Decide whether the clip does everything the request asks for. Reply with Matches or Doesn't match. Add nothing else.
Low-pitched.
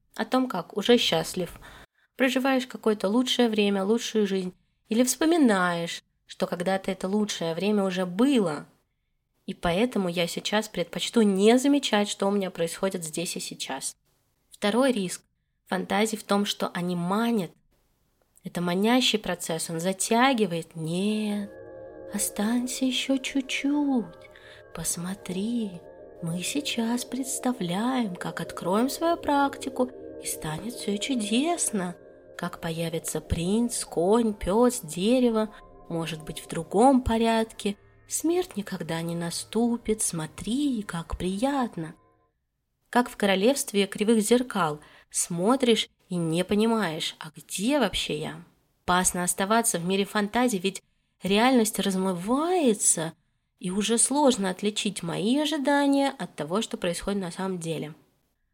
Doesn't match